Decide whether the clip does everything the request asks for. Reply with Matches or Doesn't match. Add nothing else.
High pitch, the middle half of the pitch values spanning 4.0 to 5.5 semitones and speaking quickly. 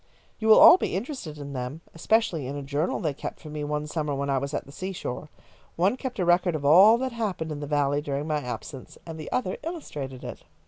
Doesn't match